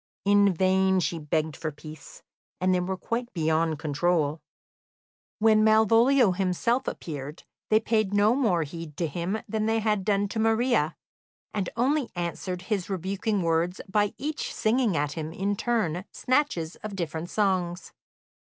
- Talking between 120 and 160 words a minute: Yes, average, 145 wpm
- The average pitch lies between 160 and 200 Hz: Yes, high, 190 Hz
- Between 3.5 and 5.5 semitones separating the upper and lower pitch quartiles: Yes, average, 4.8 semitones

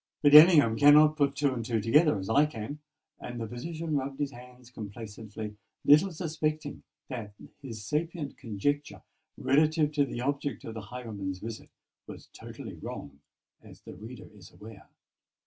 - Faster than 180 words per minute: No, average, 150 wpm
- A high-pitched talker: No, low, 130 Hz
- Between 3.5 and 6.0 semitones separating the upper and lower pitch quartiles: Yes, average, 5.1 semitones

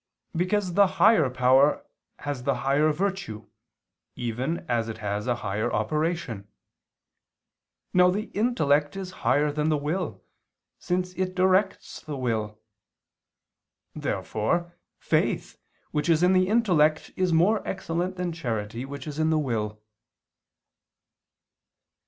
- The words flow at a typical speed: No, slow, 120 wpm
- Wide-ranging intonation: Yes, wide, 6.6 semitones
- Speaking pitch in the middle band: Yes, medium, 155 Hz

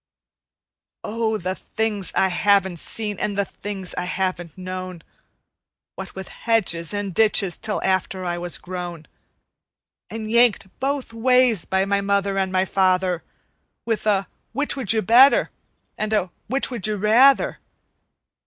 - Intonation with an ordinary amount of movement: Yes, average, 3.1 semitones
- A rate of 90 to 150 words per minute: Yes, average, 145 wpm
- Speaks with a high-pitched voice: Yes, high, 200 Hz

